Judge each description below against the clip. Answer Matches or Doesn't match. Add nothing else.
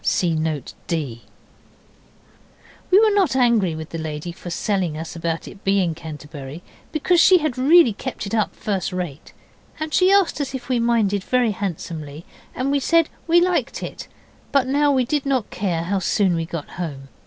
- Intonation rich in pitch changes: Matches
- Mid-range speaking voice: Doesn't match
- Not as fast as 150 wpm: Doesn't match